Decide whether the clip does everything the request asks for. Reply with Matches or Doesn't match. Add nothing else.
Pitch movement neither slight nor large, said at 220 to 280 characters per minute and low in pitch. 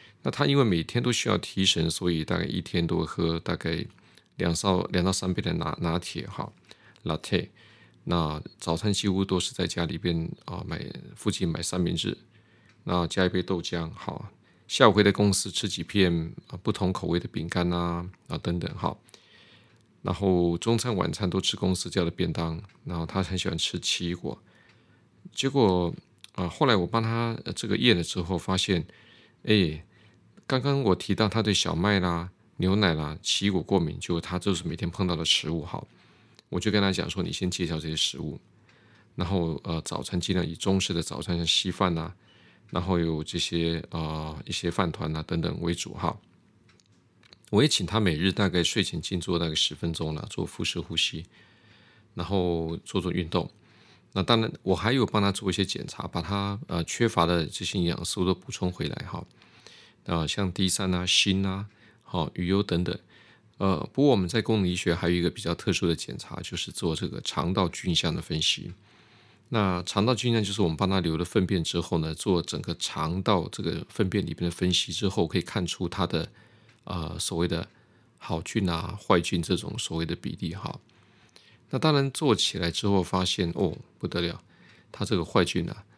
Matches